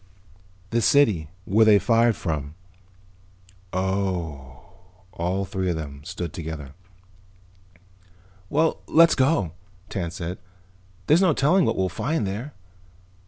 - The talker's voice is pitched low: Yes, very low, 95 Hz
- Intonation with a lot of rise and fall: Yes, wide, 6.3 semitones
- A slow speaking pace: Yes, slow, 115 wpm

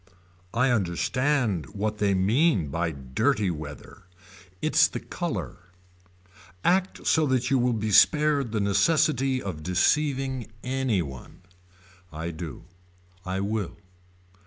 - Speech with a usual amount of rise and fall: No, wide, 7.0 semitones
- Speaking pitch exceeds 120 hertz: No, low, 105 Hz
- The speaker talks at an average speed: No, slow, 110 wpm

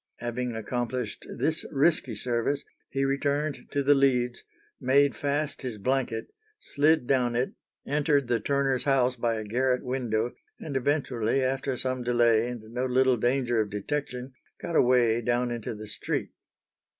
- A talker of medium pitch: No, low, 125 Hz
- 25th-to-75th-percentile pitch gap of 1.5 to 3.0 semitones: Yes, narrow, 2.5 semitones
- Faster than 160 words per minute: No, average, 150 wpm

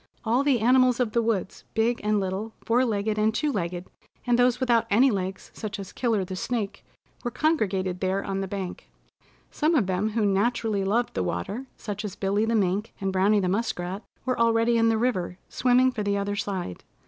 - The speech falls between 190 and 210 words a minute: Yes, average, 200 wpm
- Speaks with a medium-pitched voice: No, high, 215 Hz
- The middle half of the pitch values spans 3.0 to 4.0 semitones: Yes, average, 3.6 semitones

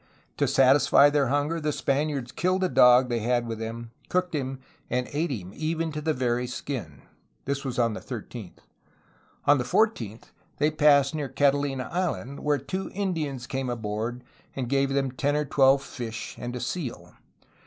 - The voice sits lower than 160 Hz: Yes, low, 135 Hz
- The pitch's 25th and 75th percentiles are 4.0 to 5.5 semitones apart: No, average, 3.4 semitones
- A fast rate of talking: No, average, 175 wpm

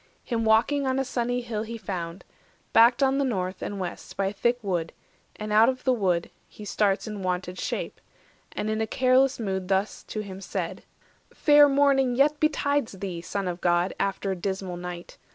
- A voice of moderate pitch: No, high, 215 Hz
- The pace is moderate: Yes, average, 190 wpm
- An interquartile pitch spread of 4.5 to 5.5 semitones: Yes, average, 5.2 semitones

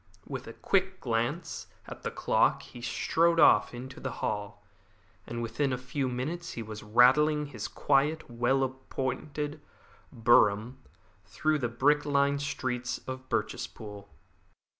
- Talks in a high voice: No, low, 130 Hz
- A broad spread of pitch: No, average, 3.7 semitones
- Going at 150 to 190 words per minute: No, average, 140 wpm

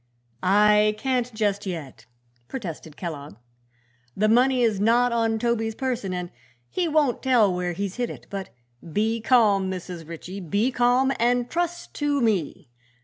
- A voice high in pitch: Yes, high, 215 Hz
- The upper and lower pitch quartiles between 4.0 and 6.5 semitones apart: Yes, average, 4.6 semitones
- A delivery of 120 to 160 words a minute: Yes, average, 145 wpm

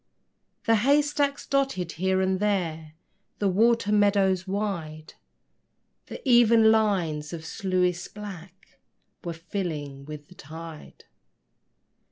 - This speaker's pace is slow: Yes, slow, 110 wpm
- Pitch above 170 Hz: Yes, high, 190 Hz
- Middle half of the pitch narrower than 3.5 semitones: No, average, 4.5 semitones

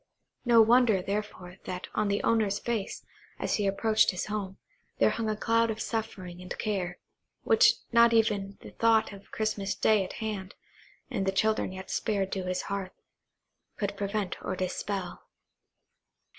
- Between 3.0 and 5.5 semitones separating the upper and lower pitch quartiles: No, narrow, 2.4 semitones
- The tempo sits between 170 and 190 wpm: No, average, 160 wpm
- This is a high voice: Yes, high, 205 Hz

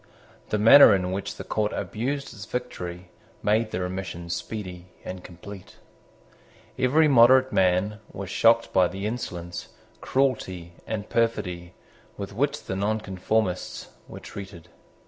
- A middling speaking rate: No, slow, 125 wpm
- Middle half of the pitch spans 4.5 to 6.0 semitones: No, average, 4.0 semitones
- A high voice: No, low, 100 Hz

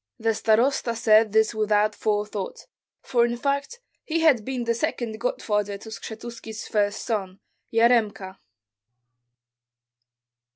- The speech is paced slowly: Yes, slow, 115 wpm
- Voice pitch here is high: Yes, high, 225 Hz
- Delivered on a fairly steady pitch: Yes, narrow, 2.2 semitones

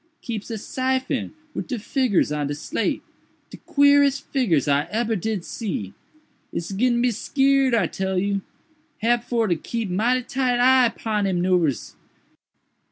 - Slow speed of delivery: No, average, 155 wpm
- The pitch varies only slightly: No, average, 5.2 semitones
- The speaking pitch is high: Yes, high, 225 Hz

